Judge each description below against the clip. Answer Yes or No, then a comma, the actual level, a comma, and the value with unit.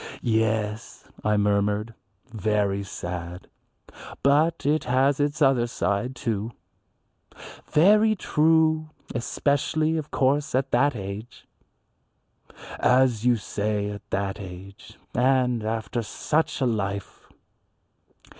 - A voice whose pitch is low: Yes, low, 120 Hz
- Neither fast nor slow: No, slow, 100 wpm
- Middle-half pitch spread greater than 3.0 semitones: Yes, wide, 5.5 semitones